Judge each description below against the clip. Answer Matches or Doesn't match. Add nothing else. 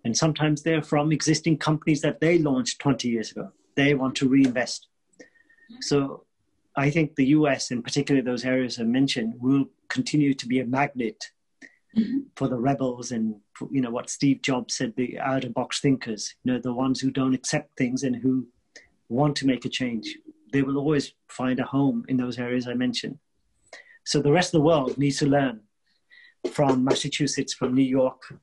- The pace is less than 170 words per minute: Doesn't match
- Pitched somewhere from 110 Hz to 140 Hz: Matches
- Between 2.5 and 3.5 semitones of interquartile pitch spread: Matches